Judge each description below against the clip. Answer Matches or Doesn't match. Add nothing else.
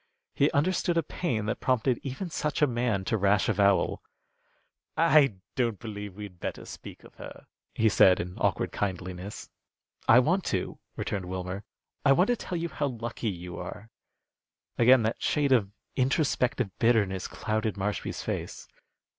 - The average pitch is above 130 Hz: Doesn't match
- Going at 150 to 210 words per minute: Matches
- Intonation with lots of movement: Matches